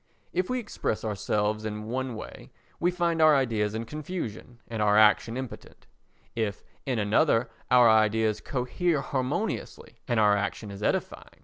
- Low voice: Yes, low, 115 Hz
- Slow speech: No, average, 150 wpm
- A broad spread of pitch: No, average, 4.0 semitones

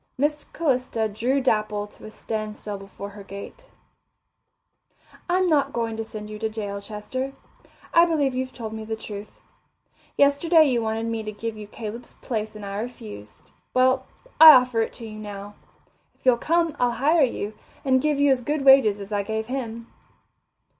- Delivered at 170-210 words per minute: Yes, average, 175 wpm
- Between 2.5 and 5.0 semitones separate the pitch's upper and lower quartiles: Yes, average, 4.0 semitones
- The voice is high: Yes, high, 225 Hz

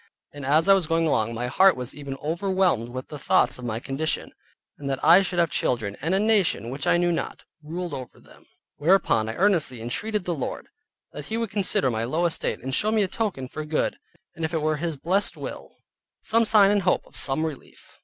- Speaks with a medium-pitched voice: Yes, medium, 160 Hz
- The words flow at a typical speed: No, fast, 225 wpm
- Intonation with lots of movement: Yes, wide, 6.2 semitones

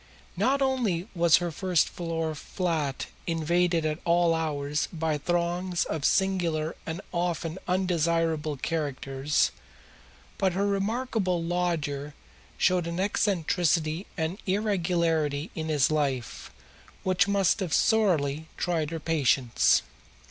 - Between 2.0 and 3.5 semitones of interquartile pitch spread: Yes, average, 2.9 semitones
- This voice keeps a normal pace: No, slow, 110 wpm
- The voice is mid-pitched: Yes, medium, 170 Hz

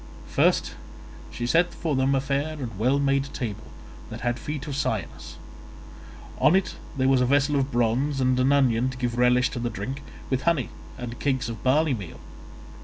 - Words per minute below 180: No, average, 185 wpm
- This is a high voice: No, low, 130 Hz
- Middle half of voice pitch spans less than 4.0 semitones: Yes, narrow, 2.6 semitones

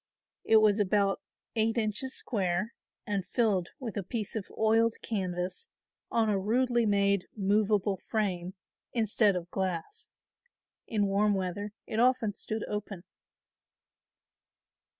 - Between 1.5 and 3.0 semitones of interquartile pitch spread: Yes, narrow, 2.5 semitones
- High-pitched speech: Yes, high, 210 Hz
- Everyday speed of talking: No, slow, 120 wpm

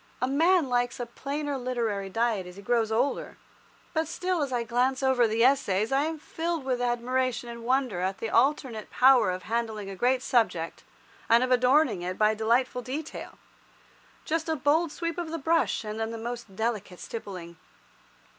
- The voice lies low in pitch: No, high, 245 Hz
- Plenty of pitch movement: No, average, 3.8 semitones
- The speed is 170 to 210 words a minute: Yes, average, 175 wpm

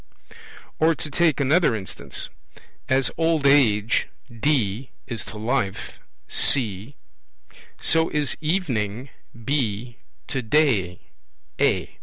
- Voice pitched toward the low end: Yes, low, 130 Hz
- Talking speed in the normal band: No, slow, 100 wpm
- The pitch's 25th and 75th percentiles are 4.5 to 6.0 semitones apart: Yes, wide, 5.6 semitones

